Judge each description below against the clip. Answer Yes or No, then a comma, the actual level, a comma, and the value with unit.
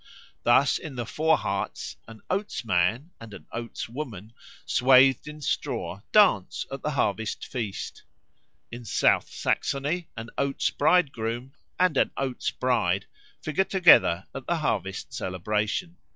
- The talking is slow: Yes, slow, 130 wpm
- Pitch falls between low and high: No, low, 125 Hz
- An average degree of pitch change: No, wide, 5.8 semitones